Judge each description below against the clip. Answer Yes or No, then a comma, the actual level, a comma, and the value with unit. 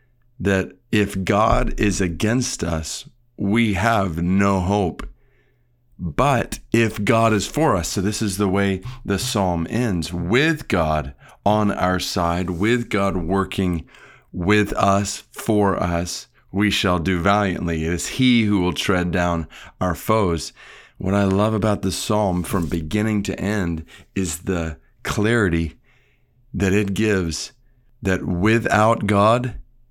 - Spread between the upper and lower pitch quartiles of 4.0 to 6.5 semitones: No, average, 3.4 semitones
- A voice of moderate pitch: No, low, 100 Hz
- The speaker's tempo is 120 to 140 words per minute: Yes, slow, 135 wpm